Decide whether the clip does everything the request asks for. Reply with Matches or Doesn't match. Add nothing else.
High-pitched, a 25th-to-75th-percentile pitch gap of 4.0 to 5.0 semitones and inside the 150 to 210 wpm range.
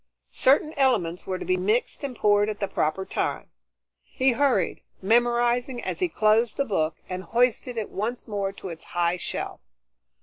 Matches